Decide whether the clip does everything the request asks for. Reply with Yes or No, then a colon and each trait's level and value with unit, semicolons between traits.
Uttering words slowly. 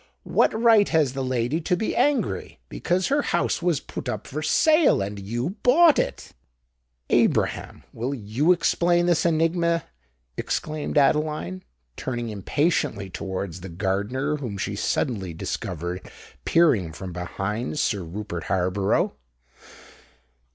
Yes: slow, 125 wpm